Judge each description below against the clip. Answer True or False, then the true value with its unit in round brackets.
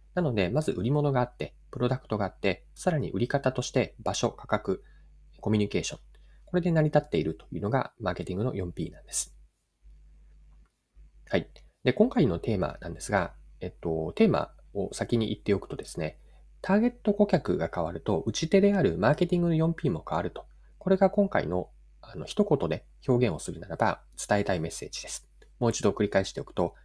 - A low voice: True (120 Hz)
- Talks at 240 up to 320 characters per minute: False (395 characters per minute)